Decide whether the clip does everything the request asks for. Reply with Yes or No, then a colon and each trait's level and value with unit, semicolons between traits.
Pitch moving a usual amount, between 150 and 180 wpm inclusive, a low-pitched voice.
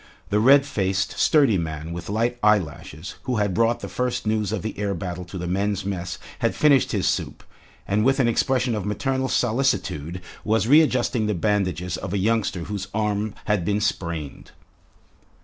Yes: average, 4.1 semitones; average, 175 wpm; low, 105 Hz